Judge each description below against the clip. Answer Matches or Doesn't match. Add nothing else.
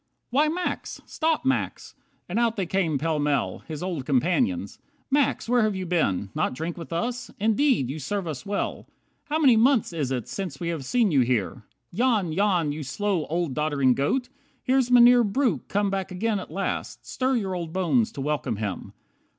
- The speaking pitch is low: Doesn't match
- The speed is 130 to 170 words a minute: Doesn't match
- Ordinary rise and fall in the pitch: Doesn't match